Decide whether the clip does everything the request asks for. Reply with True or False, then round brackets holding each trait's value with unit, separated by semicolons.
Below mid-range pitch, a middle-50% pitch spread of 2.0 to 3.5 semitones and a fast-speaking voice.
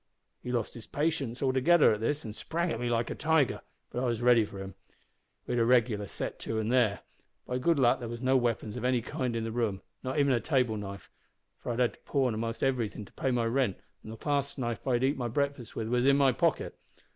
True (120 Hz; 2.7 semitones; 245 wpm)